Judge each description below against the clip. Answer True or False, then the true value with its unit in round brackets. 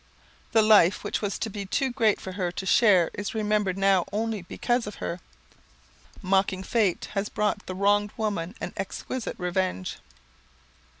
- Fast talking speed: False (160 wpm)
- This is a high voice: True (205 Hz)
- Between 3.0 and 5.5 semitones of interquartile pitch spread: False (2.4 semitones)